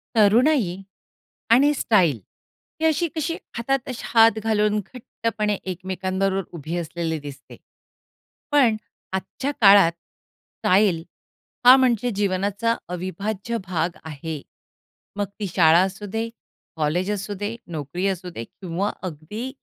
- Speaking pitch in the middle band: No, high, 195 Hz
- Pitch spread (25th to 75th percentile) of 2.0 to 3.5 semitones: No, average, 4.7 semitones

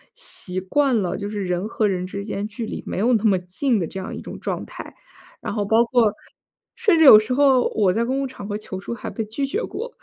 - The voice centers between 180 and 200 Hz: No, high, 215 Hz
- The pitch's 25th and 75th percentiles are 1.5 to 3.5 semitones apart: No, average, 4.6 semitones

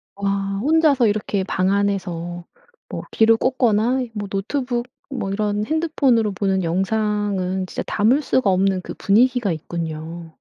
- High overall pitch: Yes, high, 205 Hz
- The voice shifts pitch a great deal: No, average, 4.1 semitones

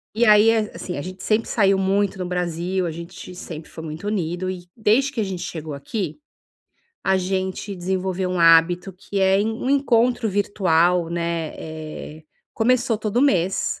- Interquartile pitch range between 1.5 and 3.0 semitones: No, average, 3.5 semitones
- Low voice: No, high, 190 Hz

